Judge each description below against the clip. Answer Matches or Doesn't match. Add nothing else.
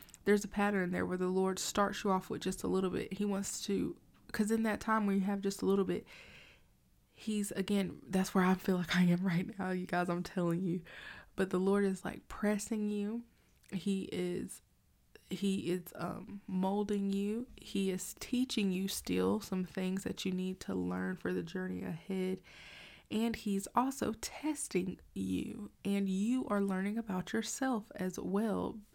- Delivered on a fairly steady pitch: Matches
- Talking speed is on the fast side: Doesn't match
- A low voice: Doesn't match